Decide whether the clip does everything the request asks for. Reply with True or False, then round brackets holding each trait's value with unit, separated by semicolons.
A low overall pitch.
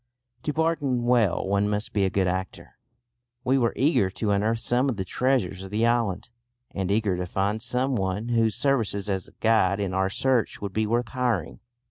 True (110 Hz)